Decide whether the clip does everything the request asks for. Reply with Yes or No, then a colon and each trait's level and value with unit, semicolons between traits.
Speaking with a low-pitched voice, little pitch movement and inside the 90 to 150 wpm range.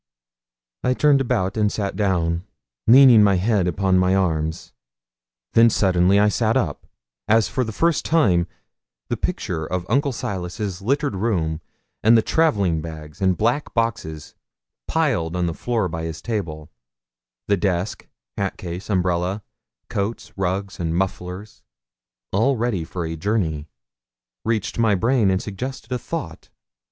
No: very low, 95 Hz; average, 4.4 semitones; average, 140 wpm